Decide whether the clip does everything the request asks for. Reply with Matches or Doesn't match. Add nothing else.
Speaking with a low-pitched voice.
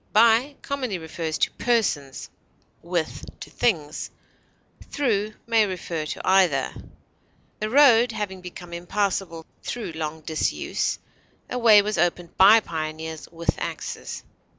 Doesn't match